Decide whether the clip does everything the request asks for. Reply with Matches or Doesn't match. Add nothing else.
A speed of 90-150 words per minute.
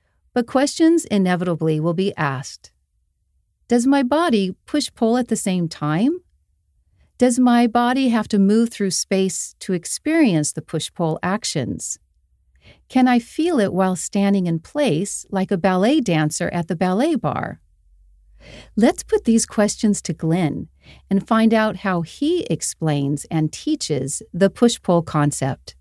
Matches